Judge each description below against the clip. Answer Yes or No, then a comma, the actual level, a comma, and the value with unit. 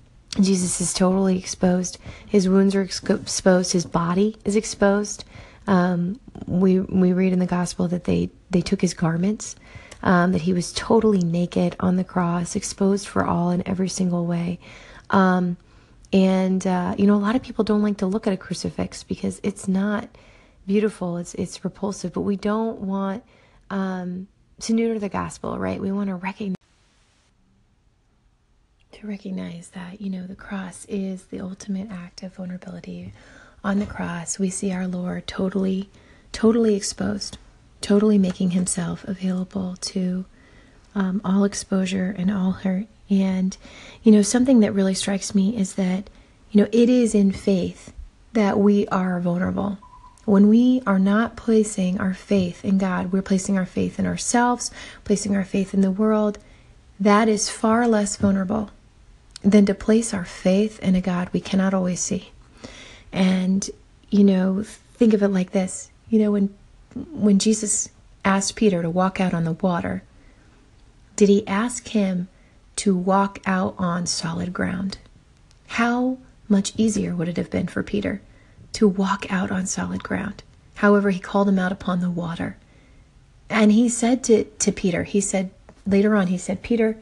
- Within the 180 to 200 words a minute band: No, average, 165 wpm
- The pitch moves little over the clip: Yes, narrow, 2.0 semitones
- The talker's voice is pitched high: Yes, high, 195 Hz